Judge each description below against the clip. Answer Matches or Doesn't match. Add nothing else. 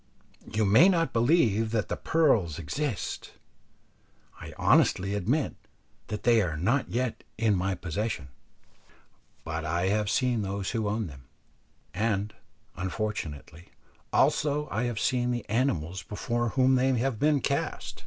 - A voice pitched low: Matches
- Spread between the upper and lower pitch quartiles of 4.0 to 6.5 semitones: Matches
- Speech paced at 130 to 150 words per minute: Matches